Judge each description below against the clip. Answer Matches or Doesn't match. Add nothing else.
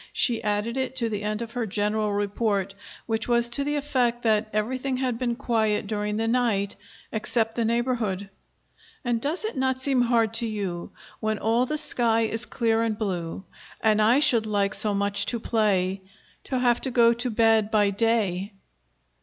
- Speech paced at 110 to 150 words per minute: Doesn't match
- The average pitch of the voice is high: Matches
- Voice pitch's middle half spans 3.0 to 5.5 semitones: Doesn't match